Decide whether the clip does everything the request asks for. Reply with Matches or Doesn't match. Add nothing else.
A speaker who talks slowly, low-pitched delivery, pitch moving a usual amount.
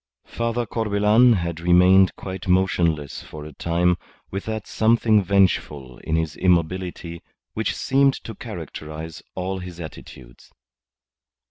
Matches